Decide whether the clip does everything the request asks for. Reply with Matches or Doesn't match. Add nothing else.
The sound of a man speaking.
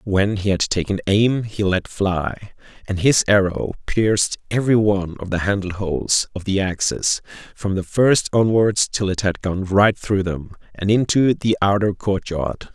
Matches